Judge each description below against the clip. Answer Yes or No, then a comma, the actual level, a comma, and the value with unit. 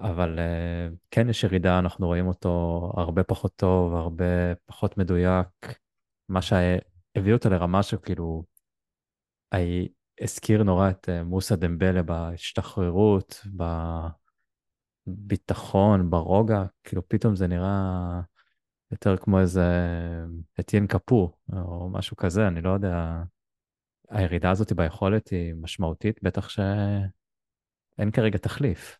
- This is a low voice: Yes, very low, 95 Hz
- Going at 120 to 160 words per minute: No, average, 105 wpm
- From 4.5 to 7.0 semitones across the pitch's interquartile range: No, average, 2.7 semitones